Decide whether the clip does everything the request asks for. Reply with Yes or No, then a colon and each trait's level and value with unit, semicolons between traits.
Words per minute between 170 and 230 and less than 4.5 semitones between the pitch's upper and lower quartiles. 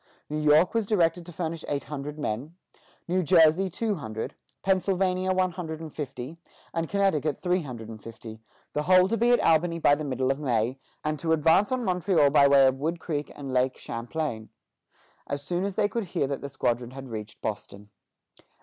No: average, 195 wpm; average, 5.2 semitones